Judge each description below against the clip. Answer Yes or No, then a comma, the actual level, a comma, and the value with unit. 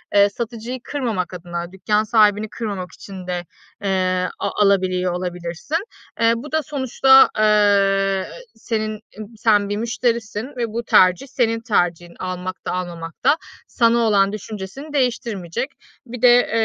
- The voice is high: Yes, high, 210 Hz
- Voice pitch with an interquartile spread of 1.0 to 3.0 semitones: No, average, 4.0 semitones